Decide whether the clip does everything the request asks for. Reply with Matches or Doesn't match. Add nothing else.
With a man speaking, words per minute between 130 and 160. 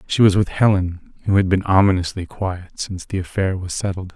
Doesn't match